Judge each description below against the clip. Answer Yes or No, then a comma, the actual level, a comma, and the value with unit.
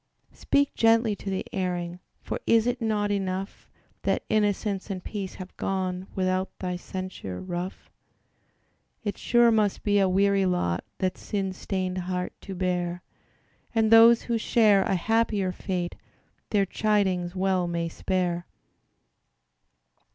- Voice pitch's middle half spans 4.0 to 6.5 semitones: No, narrow, 2.4 semitones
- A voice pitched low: No, high, 190 Hz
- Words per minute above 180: No, slow, 135 wpm